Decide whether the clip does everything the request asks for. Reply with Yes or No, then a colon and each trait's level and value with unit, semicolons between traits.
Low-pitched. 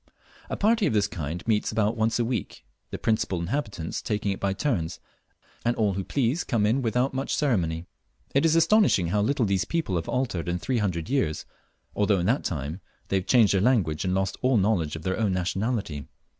Yes: low, 105 Hz